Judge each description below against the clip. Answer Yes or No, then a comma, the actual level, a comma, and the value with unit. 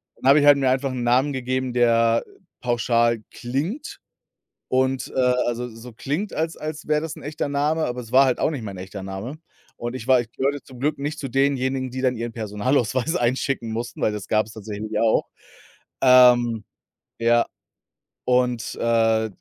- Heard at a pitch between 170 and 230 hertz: No, low, 125 Hz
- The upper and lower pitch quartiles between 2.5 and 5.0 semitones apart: Yes, average, 2.9 semitones